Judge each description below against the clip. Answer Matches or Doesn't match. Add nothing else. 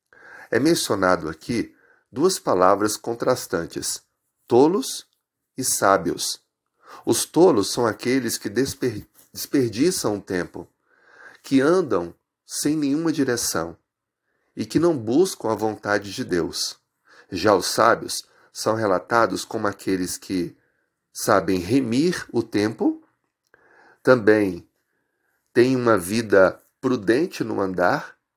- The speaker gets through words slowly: Matches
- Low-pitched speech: Matches